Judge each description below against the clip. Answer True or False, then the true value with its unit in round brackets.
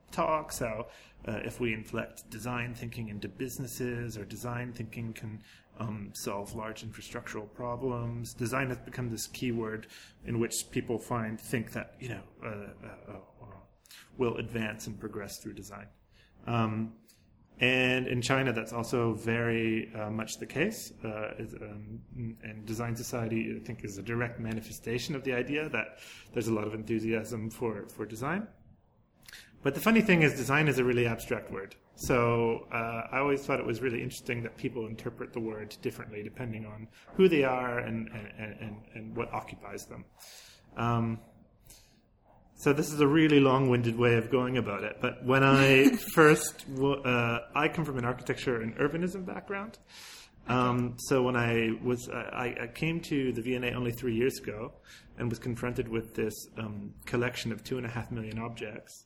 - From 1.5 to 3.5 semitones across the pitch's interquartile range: True (2.4 semitones)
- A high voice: False (115 Hz)